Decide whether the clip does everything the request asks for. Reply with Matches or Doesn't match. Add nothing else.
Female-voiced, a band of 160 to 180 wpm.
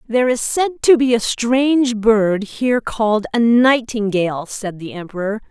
Matches